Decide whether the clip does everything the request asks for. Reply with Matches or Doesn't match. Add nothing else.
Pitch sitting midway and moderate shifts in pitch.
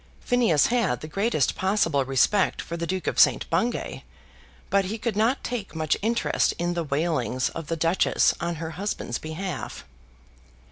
Matches